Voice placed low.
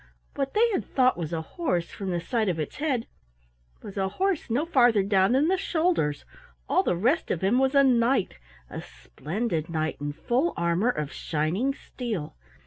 No: high, 225 Hz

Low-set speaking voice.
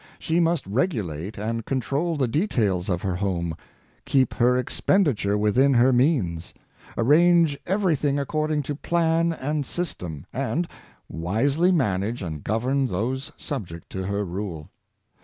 Yes: low, 125 Hz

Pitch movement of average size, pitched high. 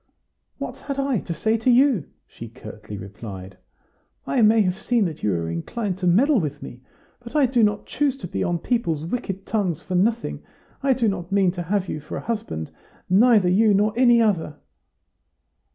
No: wide, 6.7 semitones; high, 195 Hz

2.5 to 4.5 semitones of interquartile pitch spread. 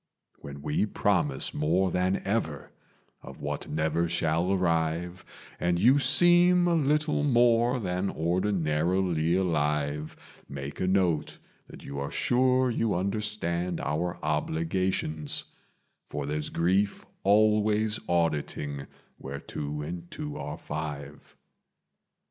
No: wide, 5.6 semitones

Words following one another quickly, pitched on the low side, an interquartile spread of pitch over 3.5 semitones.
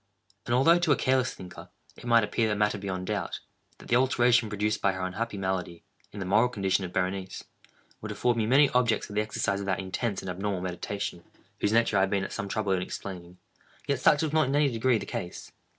Yes: fast, 230 wpm; low, 105 Hz; average, 4.1 semitones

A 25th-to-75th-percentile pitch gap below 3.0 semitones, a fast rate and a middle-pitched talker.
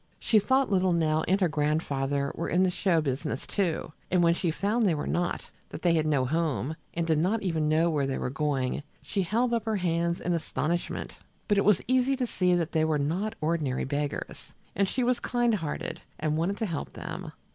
No: average, 4.5 semitones; fast, 215 wpm; medium, 170 Hz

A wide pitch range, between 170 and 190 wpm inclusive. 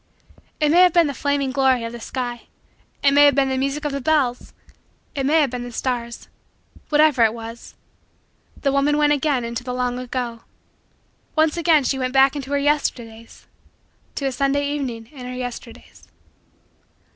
No: average, 2.9 semitones; average, 180 wpm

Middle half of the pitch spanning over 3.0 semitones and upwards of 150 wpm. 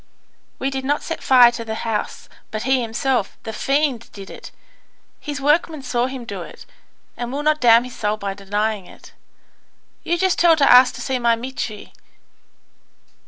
Yes: average, 3.8 semitones; average, 175 wpm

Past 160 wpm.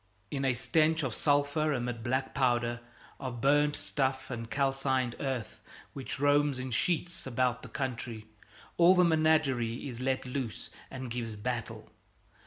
No: average, 145 wpm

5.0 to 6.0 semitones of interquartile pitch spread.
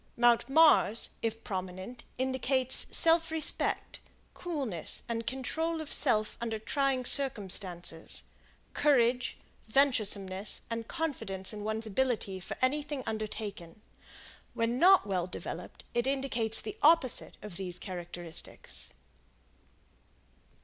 Yes: wide, 5.6 semitones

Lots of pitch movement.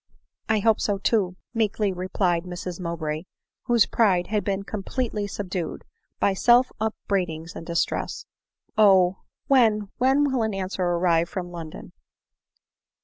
No: average, 3.7 semitones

